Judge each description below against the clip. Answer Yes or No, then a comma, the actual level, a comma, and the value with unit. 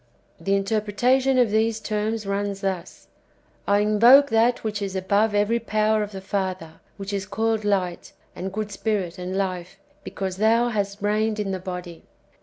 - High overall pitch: Yes, high, 205 Hz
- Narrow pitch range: Yes, narrow, 2.2 semitones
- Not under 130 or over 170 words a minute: No, average, 180 wpm